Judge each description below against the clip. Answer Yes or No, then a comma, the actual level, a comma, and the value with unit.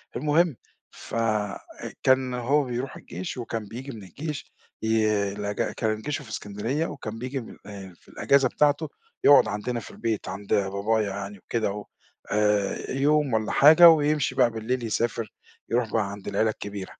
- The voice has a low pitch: Yes, low, 115 Hz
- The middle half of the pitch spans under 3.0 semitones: No, average, 4.7 semitones